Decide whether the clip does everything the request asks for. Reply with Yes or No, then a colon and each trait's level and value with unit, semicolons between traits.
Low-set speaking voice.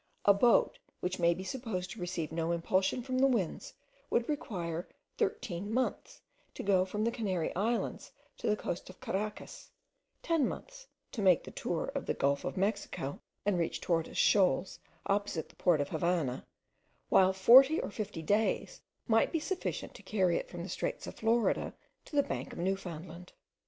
No: high, 195 Hz